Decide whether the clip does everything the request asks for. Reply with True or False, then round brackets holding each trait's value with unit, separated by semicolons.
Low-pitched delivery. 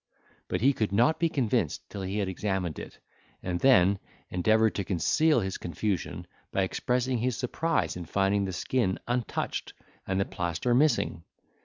True (100 Hz)